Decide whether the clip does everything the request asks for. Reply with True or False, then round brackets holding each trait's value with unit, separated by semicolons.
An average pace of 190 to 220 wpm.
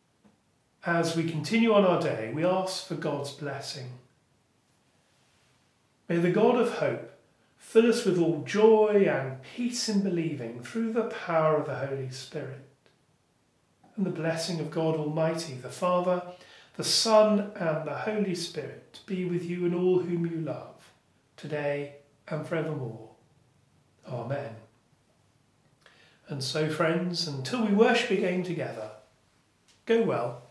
False (135 wpm)